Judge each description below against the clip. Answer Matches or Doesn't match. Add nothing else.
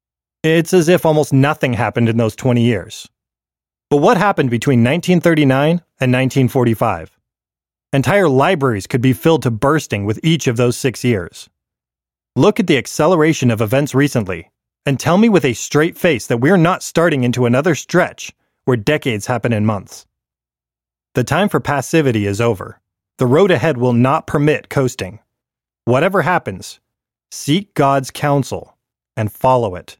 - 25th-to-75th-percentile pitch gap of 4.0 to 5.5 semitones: Matches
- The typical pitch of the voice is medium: Doesn't match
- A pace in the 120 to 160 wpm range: Matches